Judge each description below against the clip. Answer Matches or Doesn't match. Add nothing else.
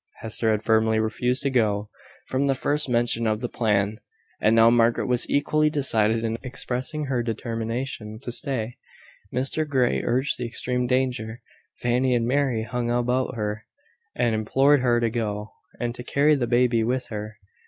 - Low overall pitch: Matches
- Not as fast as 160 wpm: Doesn't match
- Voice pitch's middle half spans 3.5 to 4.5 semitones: Doesn't match